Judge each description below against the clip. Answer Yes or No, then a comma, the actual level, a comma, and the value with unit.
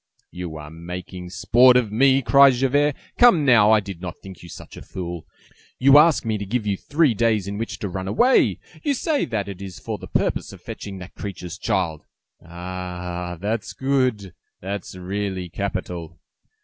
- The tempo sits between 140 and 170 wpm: No, average, 185 wpm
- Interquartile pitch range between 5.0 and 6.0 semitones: Yes, wide, 5.6 semitones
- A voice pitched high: No, low, 100 Hz